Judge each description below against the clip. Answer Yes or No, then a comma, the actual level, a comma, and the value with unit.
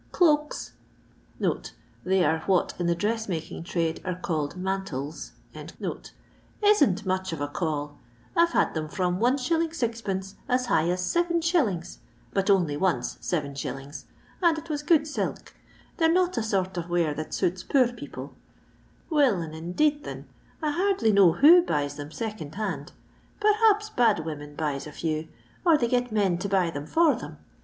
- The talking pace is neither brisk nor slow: Yes, average, 165 wpm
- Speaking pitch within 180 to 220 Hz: Yes, high, 190 Hz